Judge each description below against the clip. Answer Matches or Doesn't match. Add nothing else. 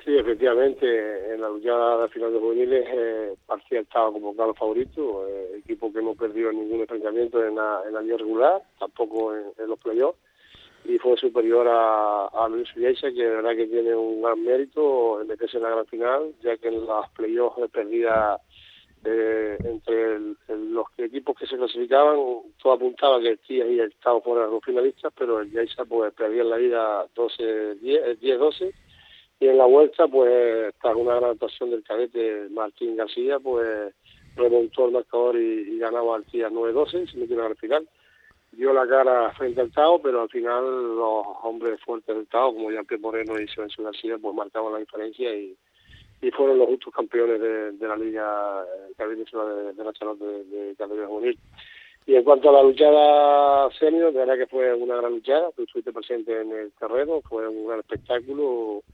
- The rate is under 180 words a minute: Doesn't match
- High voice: Doesn't match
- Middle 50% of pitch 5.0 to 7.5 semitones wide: Matches